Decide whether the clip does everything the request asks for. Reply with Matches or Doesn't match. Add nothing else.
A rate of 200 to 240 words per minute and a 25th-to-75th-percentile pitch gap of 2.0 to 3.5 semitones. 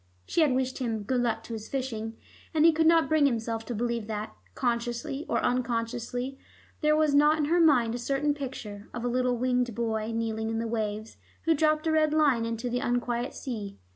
Doesn't match